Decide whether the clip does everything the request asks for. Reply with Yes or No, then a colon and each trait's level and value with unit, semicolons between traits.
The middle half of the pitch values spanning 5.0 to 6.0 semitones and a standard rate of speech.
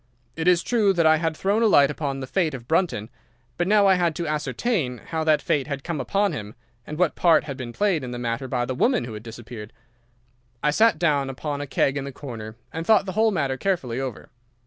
No: wide, 5.6 semitones; fast, 235 wpm